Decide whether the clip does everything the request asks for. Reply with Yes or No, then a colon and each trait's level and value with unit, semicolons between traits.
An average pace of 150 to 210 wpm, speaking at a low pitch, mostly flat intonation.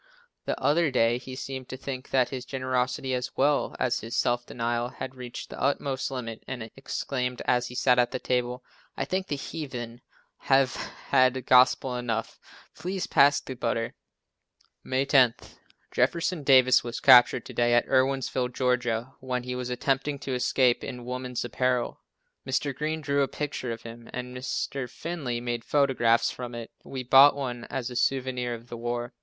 Yes: average, 170 wpm; low, 125 Hz; narrow, 1.7 semitones